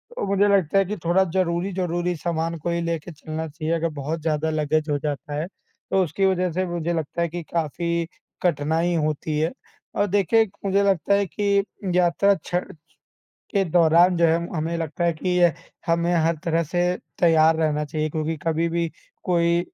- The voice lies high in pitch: No, medium, 170 Hz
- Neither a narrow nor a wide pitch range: No, narrow, 2.1 semitones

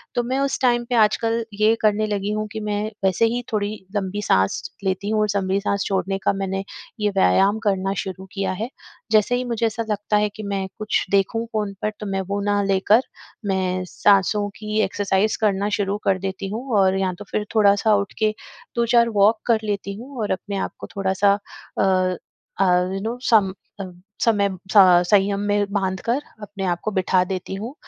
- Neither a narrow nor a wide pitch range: No, narrow, 1.9 semitones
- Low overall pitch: No, high, 205 Hz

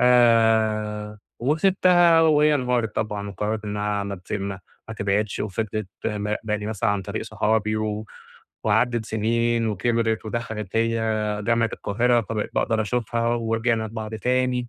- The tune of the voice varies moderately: No, narrow, 2.0 semitones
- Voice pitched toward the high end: No, low, 110 Hz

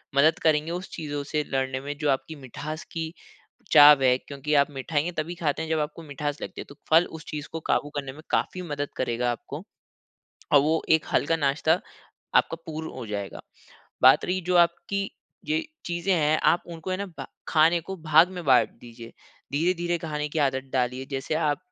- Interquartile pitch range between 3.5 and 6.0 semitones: No, average, 2.7 semitones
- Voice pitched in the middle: Yes, medium, 155 Hz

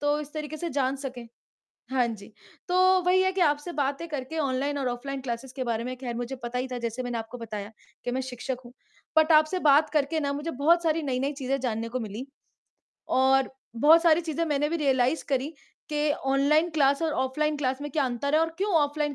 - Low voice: No, very high, 280 Hz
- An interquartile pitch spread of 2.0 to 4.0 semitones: Yes, average, 3.3 semitones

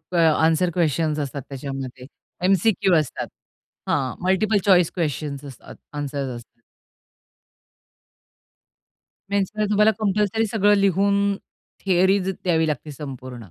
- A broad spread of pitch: Yes, wide, 6.0 semitones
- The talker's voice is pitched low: No, medium, 175 Hz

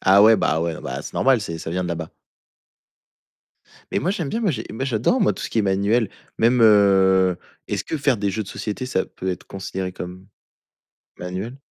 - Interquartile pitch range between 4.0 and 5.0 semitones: Yes, average, 4.5 semitones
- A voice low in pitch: Yes, low, 100 Hz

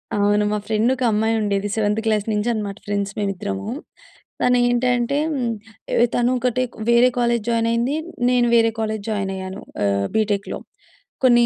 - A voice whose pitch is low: No, high, 220 Hz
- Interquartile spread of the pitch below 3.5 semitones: Yes, average, 2.8 semitones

